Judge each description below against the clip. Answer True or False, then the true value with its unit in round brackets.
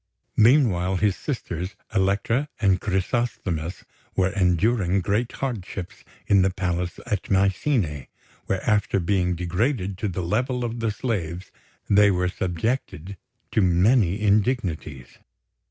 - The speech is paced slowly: True (120 wpm)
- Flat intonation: False (3.7 semitones)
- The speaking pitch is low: True (95 Hz)